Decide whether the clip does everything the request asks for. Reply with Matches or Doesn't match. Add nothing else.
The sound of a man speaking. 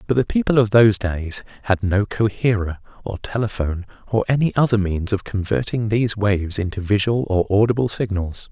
Matches